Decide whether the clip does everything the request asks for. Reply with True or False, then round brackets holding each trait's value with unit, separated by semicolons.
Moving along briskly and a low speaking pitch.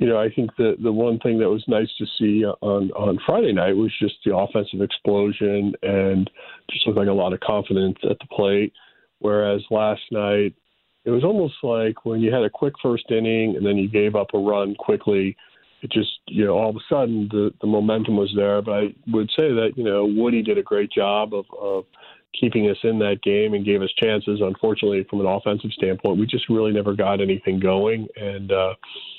True (215 wpm; 105 Hz)